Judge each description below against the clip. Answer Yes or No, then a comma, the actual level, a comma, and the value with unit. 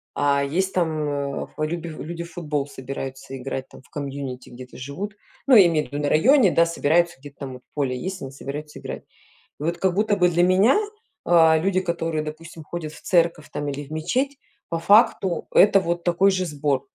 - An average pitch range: Yes, average, 3.9 semitones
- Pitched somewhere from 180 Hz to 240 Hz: No, medium, 160 Hz